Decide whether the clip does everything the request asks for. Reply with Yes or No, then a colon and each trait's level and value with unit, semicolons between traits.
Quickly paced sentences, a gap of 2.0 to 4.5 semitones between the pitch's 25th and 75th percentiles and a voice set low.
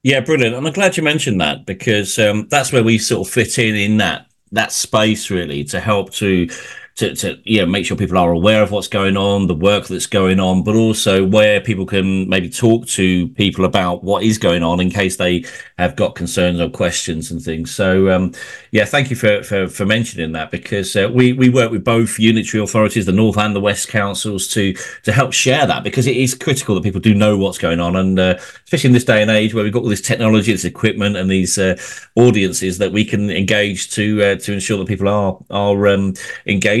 Yes: fast, 230 wpm; average, 2.9 semitones; low, 105 Hz